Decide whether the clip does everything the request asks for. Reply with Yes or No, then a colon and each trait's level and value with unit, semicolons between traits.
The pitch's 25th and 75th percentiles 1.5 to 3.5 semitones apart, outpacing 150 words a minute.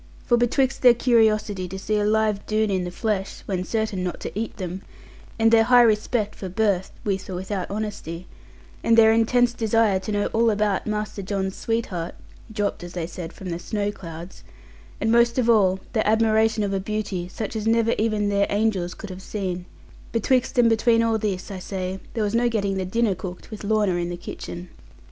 Yes: average, 3.0 semitones; average, 200 wpm